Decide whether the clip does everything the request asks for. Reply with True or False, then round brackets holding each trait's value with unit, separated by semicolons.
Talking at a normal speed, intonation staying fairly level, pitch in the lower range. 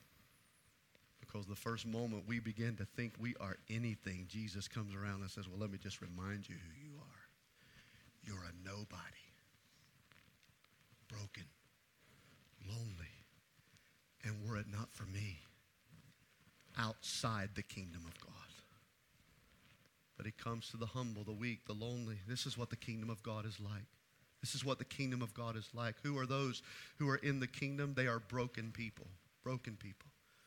False (160 wpm; 3.0 semitones; 110 Hz)